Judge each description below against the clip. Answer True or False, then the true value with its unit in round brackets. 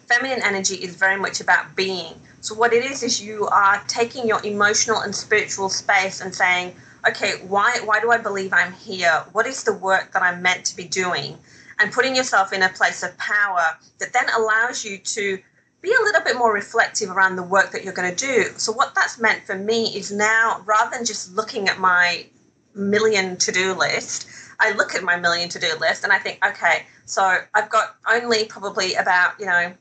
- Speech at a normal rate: False (210 wpm)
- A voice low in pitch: False (205 Hz)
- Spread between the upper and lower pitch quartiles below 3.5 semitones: True (3.1 semitones)